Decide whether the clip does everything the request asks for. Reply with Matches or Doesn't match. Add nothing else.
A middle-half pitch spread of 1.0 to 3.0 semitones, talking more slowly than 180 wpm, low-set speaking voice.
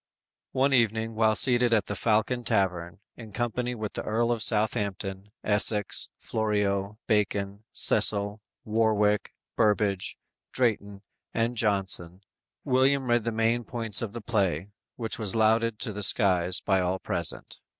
Matches